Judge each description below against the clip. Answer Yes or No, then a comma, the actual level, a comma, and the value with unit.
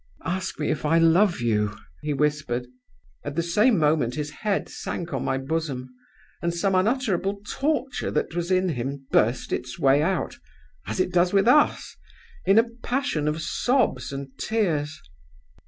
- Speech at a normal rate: Yes, average, 160 wpm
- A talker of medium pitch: Yes, medium, 165 Hz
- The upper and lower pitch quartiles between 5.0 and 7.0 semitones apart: Yes, wide, 5.6 semitones